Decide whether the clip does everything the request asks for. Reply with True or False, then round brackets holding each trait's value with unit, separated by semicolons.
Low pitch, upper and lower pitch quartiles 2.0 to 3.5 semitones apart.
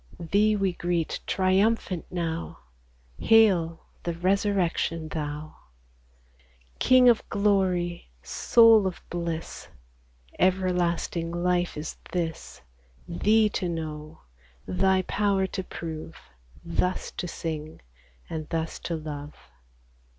False (175 Hz; 2.9 semitones)